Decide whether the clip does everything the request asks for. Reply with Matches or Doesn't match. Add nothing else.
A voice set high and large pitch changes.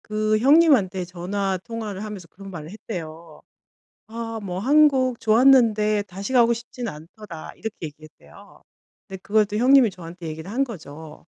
Doesn't match